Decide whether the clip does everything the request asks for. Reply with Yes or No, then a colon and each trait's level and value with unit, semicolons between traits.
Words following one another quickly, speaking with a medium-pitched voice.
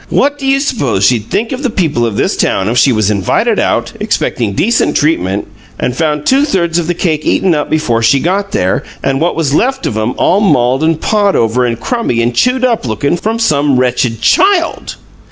Yes: fast, 210 wpm; medium, 150 Hz